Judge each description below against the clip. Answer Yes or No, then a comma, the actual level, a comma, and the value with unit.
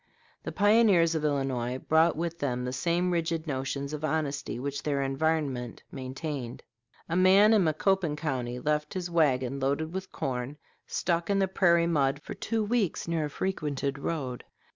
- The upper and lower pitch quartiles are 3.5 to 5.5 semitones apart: Yes, average, 3.9 semitones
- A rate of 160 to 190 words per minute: Yes, average, 165 wpm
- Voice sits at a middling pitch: Yes, medium, 155 Hz